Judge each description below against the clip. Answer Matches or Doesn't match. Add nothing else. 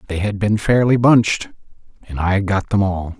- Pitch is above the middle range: Doesn't match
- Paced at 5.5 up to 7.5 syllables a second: Doesn't match